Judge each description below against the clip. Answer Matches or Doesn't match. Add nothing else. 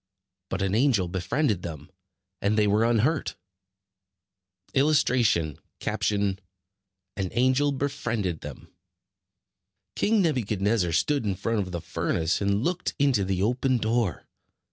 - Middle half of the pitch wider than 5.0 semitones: Matches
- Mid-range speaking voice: Doesn't match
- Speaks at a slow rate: Matches